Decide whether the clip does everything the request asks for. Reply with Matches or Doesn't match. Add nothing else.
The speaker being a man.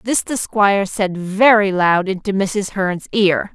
Doesn't match